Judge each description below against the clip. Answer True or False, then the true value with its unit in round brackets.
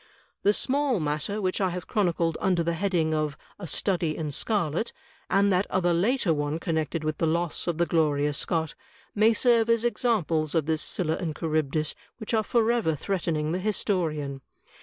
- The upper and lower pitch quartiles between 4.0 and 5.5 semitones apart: True (4.6 semitones)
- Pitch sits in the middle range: True (170 Hz)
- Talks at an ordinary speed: True (175 wpm)